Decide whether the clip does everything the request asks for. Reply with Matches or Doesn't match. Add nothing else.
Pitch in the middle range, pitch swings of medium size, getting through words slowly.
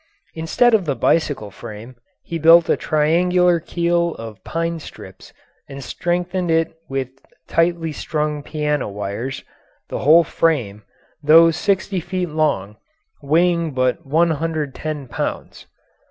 Matches